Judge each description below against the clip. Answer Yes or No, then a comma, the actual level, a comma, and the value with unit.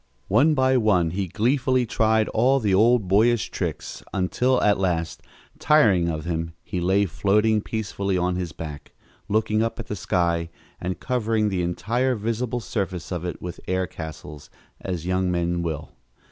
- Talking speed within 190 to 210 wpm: No, average, 160 wpm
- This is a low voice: Yes, low, 100 Hz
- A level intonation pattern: No, average, 4.3 semitones